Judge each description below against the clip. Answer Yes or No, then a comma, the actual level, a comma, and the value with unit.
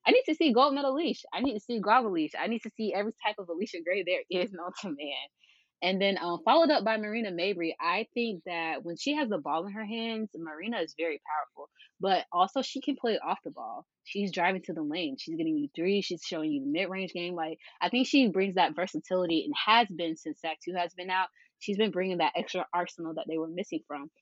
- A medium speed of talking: No, fast, 250 wpm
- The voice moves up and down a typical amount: No, wide, 6.4 semitones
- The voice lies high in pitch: Yes, high, 195 Hz